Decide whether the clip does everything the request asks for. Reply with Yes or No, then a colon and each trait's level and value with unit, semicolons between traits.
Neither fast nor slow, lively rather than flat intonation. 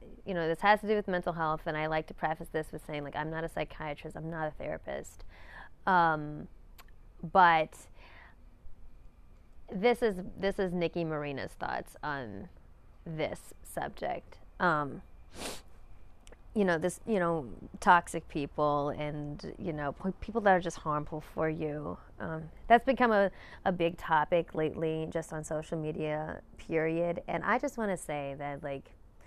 No: average, 160 wpm; average, 3.3 semitones